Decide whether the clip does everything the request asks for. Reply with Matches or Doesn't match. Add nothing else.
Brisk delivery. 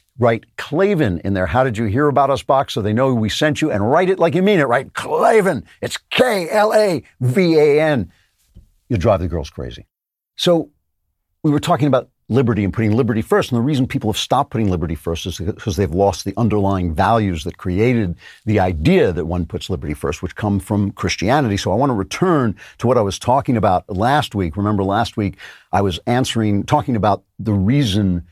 Matches